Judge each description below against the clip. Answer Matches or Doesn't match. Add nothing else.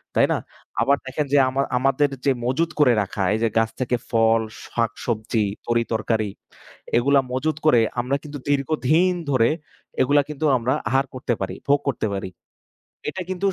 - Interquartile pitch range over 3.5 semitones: Matches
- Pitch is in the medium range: Doesn't match